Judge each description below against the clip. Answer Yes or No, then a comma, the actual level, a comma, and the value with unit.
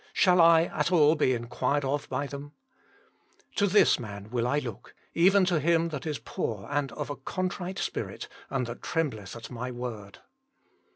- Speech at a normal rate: Yes, average, 185 wpm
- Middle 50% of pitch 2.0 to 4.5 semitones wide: No, wide, 5.5 semitones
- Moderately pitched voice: Yes, medium, 145 Hz